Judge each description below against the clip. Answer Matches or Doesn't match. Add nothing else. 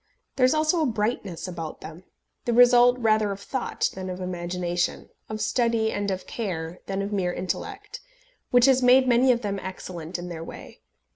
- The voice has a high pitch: Matches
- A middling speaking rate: Matches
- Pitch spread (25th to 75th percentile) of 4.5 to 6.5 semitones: Matches